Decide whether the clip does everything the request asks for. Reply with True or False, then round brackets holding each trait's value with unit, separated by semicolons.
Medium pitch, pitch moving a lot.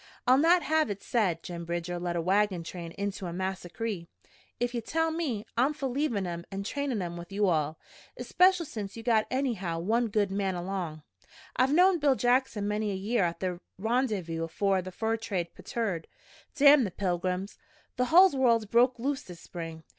False (205 Hz; 6.0 semitones)